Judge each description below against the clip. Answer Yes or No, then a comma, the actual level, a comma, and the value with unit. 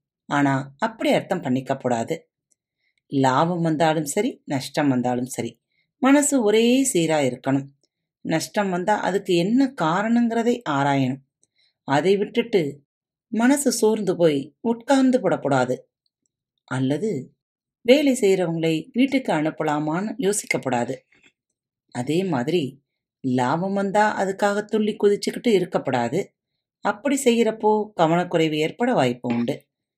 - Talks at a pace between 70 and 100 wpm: Yes, average, 95 wpm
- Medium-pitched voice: Yes, medium, 175 Hz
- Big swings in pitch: Yes, wide, 7.6 semitones